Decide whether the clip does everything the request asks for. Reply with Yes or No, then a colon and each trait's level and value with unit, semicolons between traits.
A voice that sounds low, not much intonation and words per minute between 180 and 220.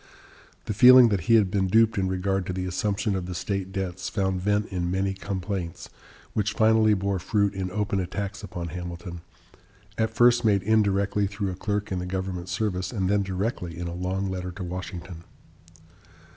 Yes: very low, 95 Hz; narrow, 2.2 semitones; average, 185 wpm